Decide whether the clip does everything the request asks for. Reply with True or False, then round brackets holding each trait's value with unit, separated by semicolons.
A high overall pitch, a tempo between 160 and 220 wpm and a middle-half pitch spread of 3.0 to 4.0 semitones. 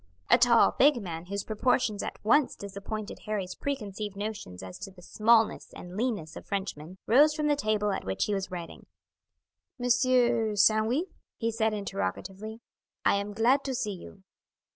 True (215 Hz; 165 wpm; 3.7 semitones)